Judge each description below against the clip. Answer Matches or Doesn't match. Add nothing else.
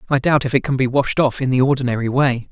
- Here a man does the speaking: Matches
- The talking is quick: Matches